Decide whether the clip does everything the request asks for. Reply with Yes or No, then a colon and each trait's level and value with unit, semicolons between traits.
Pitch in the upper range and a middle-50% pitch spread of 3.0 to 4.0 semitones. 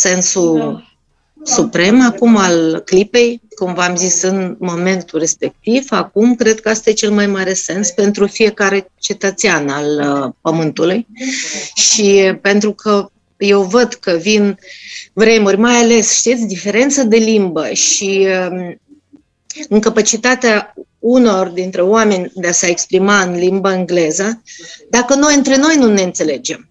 Yes: high, 205 Hz; average, 3.7 semitones